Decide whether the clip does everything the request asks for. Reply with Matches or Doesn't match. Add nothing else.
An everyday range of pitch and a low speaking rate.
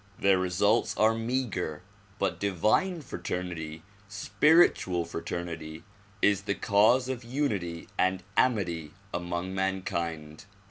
Matches